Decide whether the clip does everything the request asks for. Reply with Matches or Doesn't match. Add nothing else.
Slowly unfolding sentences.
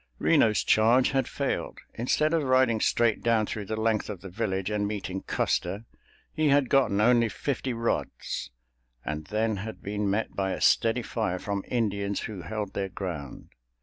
Doesn't match